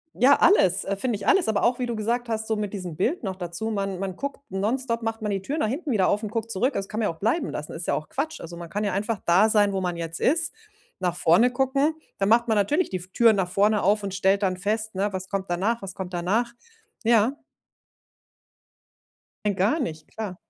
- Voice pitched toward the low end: No, high, 210 Hz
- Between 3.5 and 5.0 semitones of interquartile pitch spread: Yes, average, 3.8 semitones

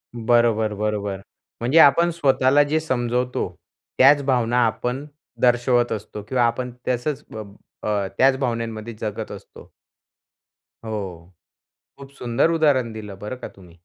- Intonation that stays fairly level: No, average, 3.2 semitones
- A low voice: Yes, low, 120 Hz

